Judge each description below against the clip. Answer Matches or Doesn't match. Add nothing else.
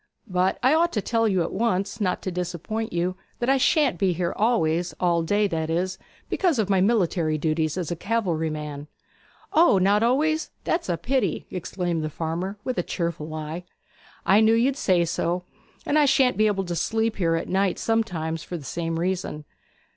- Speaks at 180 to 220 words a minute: Matches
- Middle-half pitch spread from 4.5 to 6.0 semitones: Matches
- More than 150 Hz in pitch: Matches